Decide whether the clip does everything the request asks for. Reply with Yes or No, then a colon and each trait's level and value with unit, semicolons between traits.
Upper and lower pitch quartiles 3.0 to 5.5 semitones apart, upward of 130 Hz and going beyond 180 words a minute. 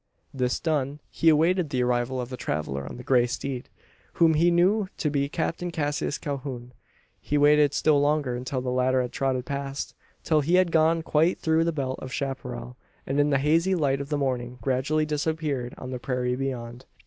Yes: average, 3.4 semitones; medium, 140 Hz; average, 195 wpm